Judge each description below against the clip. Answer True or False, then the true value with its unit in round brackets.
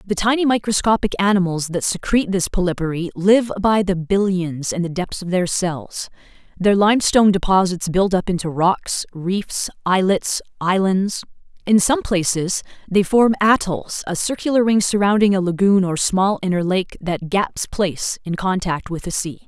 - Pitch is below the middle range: False (190 Hz)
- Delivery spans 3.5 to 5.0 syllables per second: True (4.7 syllables/s)